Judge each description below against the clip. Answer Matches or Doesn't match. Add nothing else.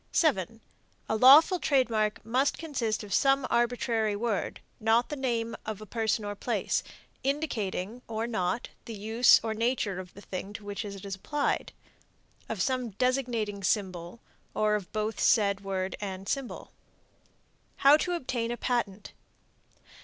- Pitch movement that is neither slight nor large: Matches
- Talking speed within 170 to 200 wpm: Doesn't match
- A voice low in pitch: Doesn't match